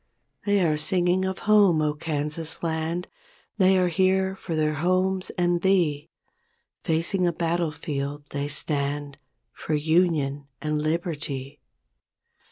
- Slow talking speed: Yes, slow, 130 wpm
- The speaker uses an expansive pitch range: No, average, 3.5 semitones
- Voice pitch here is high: No, medium, 160 Hz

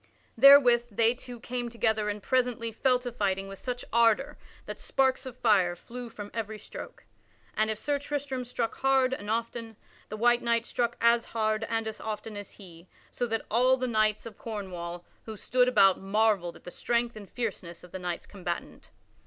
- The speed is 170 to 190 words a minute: Yes, average, 185 wpm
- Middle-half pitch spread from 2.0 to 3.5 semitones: Yes, average, 3.0 semitones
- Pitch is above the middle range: Yes, high, 225 Hz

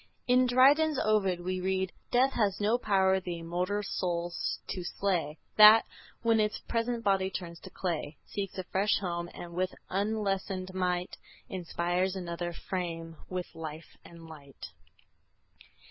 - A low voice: No, medium, 185 Hz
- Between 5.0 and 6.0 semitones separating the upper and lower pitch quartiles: No, average, 3.1 semitones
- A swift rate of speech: No, average, 140 wpm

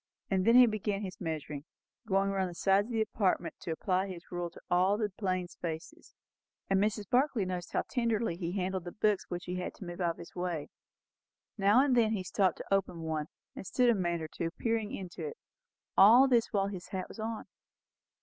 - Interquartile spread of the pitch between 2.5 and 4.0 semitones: Yes, average, 3.6 semitones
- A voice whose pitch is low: No, high, 195 Hz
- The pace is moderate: No, fast, 215 wpm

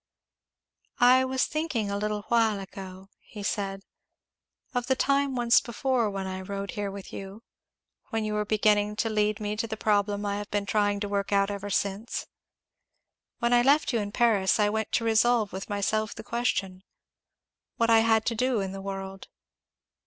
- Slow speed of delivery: No, average, 180 wpm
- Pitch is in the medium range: No, high, 210 Hz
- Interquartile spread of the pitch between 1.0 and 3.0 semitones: Yes, narrow, 2.5 semitones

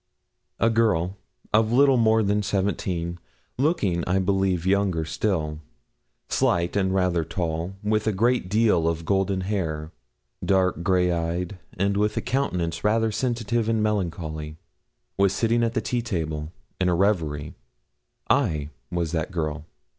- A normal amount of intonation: Yes, average, 4.3 semitones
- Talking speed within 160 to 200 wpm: No, average, 145 wpm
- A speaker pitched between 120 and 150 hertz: No, very low, 95 Hz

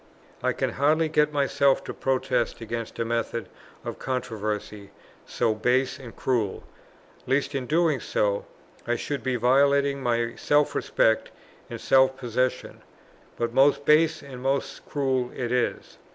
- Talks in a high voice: No, low, 130 Hz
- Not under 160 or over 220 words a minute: No, average, 140 wpm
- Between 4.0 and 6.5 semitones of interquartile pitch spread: No, average, 3.1 semitones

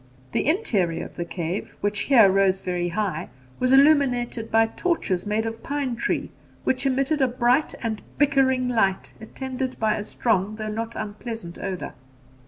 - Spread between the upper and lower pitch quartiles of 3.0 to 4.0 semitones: No, average, 4.4 semitones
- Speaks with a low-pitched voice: No, high, 225 Hz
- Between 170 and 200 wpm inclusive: No, average, 160 wpm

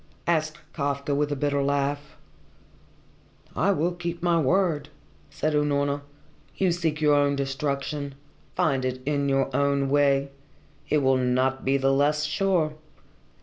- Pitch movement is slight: Yes, narrow, 1.8 semitones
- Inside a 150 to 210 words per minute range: No, average, 140 wpm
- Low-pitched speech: No, medium, 145 Hz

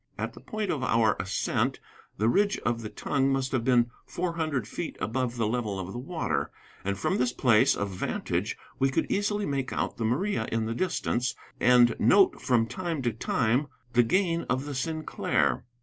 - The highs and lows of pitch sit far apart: Yes, wide, 5.7 semitones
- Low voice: Yes, low, 125 Hz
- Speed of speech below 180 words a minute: No, average, 190 wpm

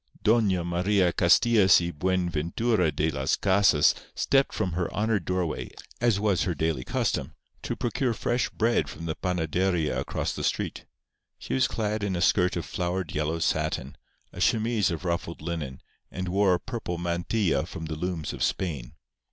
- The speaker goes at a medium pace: Yes, average, 165 wpm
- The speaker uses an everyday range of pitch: Yes, average, 3.9 semitones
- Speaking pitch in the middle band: No, very low, 90 Hz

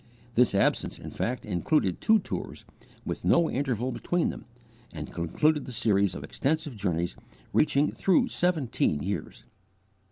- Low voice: Yes, low, 125 Hz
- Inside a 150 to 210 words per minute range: No, slow, 135 wpm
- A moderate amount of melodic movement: No, wide, 8.3 semitones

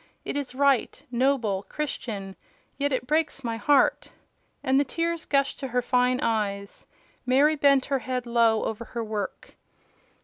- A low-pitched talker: No, very high, 255 Hz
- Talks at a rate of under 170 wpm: Yes, average, 150 wpm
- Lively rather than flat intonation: No, average, 3.7 semitones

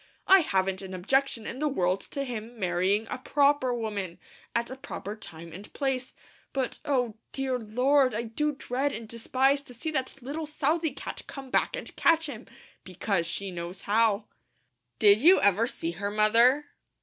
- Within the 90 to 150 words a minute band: No, average, 175 wpm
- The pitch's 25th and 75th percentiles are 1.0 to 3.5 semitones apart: No, average, 5.3 semitones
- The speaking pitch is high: Yes, high, 235 Hz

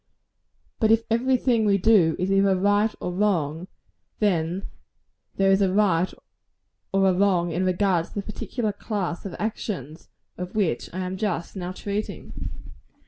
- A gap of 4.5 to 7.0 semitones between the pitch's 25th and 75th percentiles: No, average, 2.7 semitones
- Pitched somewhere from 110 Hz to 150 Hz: No, high, 195 Hz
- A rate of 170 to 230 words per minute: No, average, 155 wpm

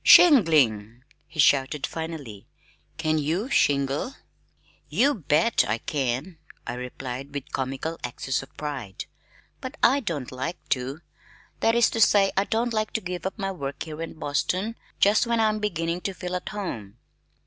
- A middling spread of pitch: No, wide, 7.1 semitones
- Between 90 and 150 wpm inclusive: No, average, 160 wpm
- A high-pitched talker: No, medium, 160 Hz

